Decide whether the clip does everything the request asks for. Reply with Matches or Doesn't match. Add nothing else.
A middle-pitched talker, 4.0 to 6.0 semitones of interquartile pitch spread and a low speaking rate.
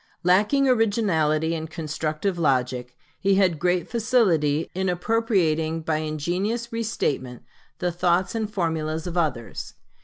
Matches